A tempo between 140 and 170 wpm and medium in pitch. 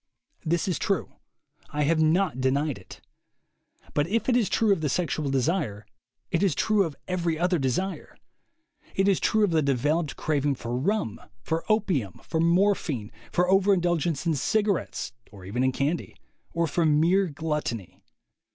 Yes: average, 160 wpm; medium, 160 Hz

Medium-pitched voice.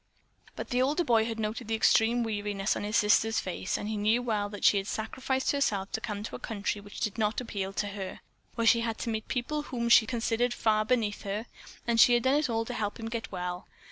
No: high, 225 Hz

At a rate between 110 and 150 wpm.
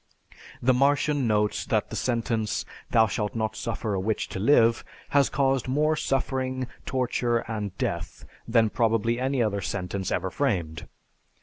Yes: average, 145 wpm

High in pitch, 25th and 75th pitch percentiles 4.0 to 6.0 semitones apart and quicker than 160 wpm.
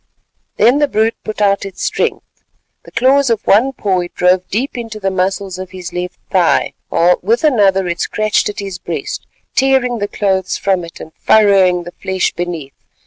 No: high, 195 Hz; average, 3.4 semitones; average, 185 wpm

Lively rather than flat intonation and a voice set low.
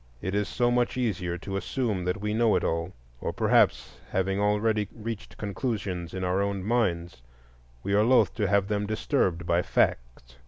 No: average, 3.3 semitones; low, 100 Hz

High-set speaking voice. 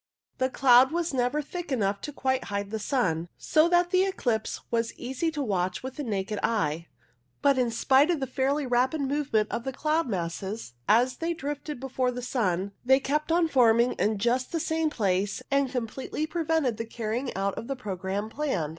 Yes: very high, 255 Hz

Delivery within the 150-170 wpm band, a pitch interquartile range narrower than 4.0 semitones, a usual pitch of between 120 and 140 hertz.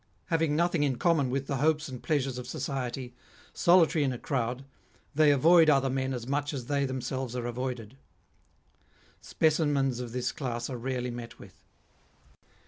Yes: average, 160 wpm; average, 2.8 semitones; low, 135 Hz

